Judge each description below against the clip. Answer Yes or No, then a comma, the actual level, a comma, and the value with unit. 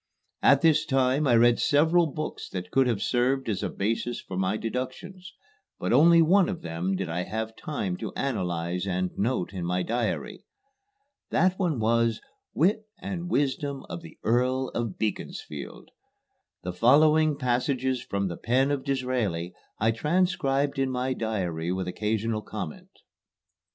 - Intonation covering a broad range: Yes, wide, 6.5 semitones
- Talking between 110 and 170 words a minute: Yes, average, 150 wpm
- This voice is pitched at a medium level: No, low, 125 Hz